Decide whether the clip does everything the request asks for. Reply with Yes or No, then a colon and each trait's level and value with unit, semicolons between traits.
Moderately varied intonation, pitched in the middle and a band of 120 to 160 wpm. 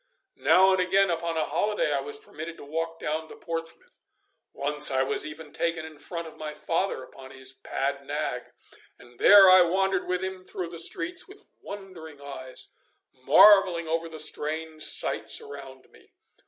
No: average, 3.7 semitones; medium, 165 Hz; average, 170 wpm